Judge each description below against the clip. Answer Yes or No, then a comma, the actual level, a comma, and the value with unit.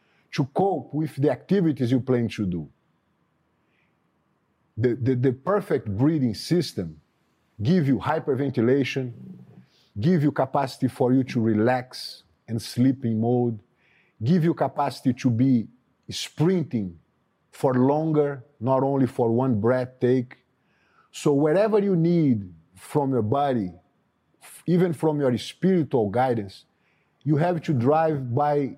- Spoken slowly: Yes, slow, 125 wpm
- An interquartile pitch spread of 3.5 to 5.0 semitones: Yes, average, 4.1 semitones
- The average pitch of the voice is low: Yes, low, 130 Hz